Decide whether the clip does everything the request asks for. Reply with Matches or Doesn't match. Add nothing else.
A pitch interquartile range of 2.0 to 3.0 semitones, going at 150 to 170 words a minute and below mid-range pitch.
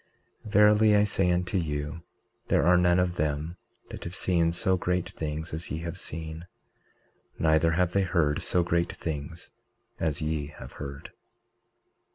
Matches